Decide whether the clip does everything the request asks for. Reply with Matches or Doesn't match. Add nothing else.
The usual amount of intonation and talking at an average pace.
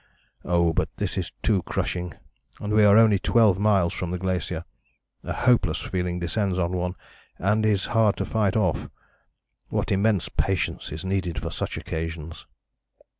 Matches